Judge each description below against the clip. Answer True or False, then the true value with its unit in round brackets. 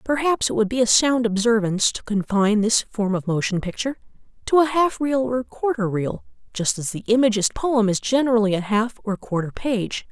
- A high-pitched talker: True (225 Hz)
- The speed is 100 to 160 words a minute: False (195 wpm)